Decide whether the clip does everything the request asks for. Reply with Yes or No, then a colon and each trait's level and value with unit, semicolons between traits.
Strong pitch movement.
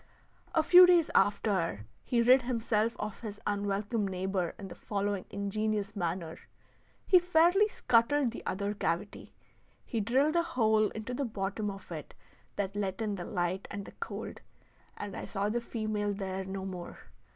No: average, 3.3 semitones